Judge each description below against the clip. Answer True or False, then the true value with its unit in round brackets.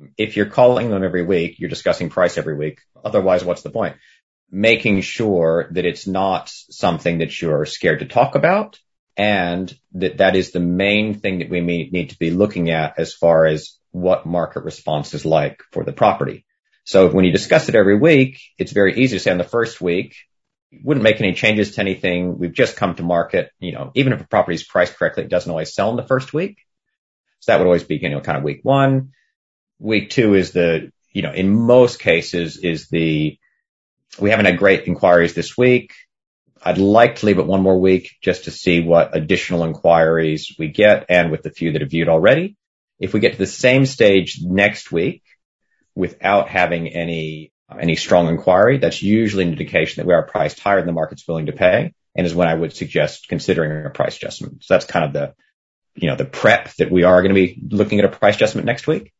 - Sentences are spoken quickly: True (215 wpm)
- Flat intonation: False (3.7 semitones)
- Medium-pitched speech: False (90 Hz)